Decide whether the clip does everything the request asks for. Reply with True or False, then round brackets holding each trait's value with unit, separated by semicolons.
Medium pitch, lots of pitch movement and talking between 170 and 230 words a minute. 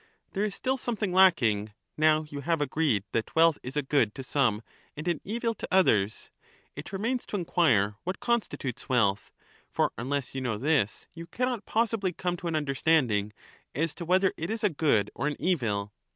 True (155 Hz; 7.4 semitones; 185 wpm)